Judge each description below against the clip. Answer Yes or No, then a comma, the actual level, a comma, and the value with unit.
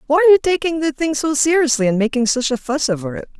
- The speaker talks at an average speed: No, fast, 265 wpm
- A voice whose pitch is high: Yes, very high, 280 Hz